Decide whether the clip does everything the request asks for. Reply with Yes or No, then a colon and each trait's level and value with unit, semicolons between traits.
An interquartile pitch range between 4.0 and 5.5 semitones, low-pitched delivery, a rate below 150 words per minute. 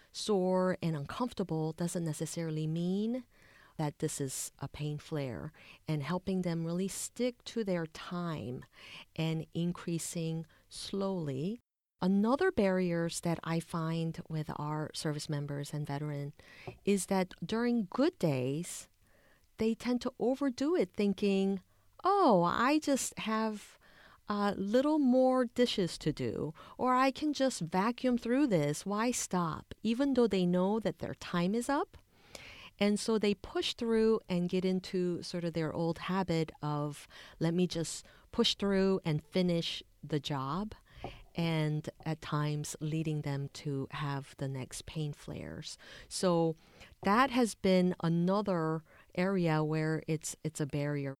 No: average, 5.2 semitones; medium, 175 Hz; average, 140 wpm